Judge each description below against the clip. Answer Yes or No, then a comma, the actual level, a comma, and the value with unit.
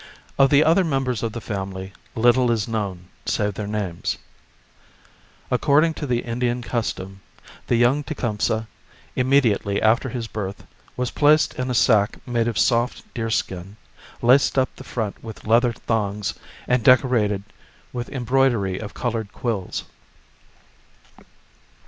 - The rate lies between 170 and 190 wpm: No, slow, 135 wpm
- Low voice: Yes, low, 115 Hz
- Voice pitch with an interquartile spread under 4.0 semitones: Yes, average, 3.5 semitones